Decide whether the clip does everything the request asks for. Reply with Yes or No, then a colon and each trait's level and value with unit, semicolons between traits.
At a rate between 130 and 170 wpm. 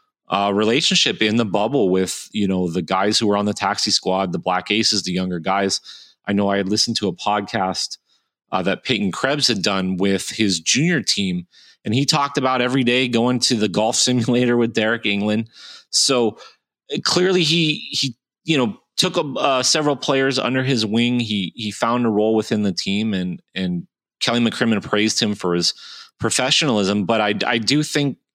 No: average, 190 wpm